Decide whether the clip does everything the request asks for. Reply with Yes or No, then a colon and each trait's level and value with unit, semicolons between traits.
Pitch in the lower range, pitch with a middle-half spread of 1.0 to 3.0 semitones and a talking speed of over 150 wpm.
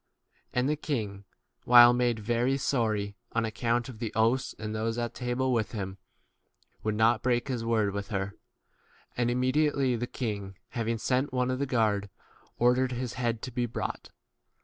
Yes: low, 120 Hz; narrow, 2.6 semitones; average, 175 wpm